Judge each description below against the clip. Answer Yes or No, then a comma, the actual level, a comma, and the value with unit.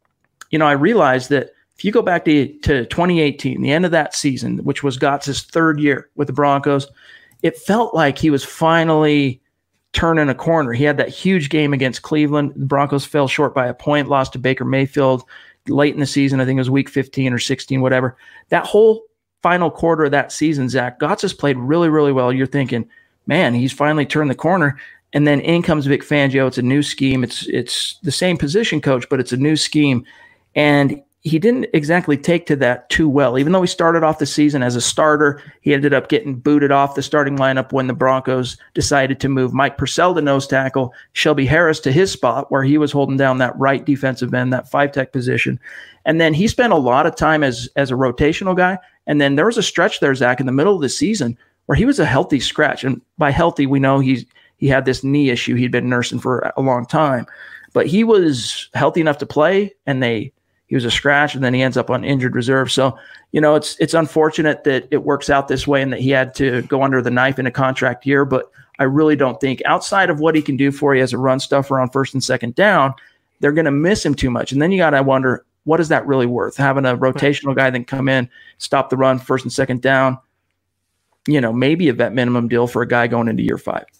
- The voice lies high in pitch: No, medium, 140 Hz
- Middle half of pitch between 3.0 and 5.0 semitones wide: No, narrow, 2.6 semitones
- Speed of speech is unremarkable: No, fast, 235 wpm